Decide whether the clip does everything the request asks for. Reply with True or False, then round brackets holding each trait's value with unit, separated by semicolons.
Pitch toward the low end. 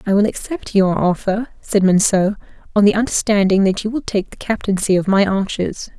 False (200 Hz)